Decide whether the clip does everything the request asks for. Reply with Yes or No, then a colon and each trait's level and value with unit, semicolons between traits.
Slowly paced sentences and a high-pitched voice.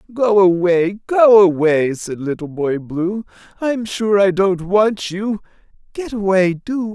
Yes: slow, 130 wpm; high, 195 Hz